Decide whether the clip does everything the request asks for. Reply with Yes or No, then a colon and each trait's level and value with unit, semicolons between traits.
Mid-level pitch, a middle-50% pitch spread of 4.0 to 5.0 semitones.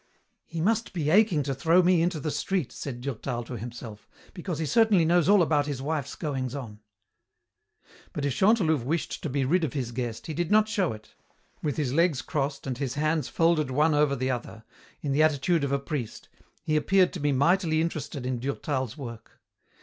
Yes: medium, 150 Hz; average, 4.3 semitones